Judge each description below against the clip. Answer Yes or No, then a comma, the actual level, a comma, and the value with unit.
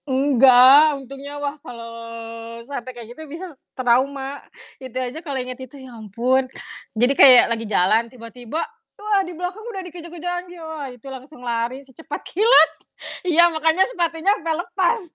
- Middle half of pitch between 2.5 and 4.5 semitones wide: No, average, 5.0 semitones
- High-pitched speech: Yes, very high, 275 Hz